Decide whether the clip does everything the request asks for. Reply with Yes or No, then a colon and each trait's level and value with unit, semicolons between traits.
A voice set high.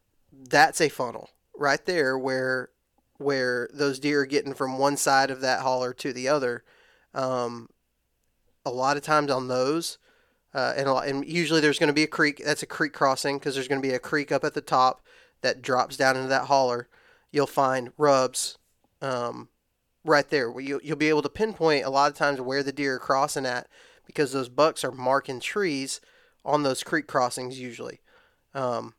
No: low, 135 Hz